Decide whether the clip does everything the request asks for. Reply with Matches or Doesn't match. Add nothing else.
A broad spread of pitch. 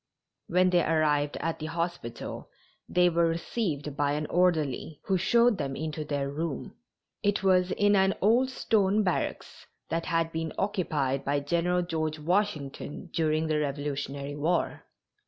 Doesn't match